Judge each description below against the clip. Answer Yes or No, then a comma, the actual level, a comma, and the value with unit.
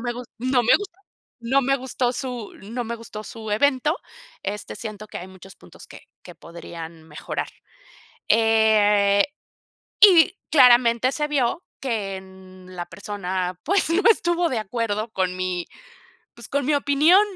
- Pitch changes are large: Yes, wide, 5.9 semitones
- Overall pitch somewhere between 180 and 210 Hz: No, high, 230 Hz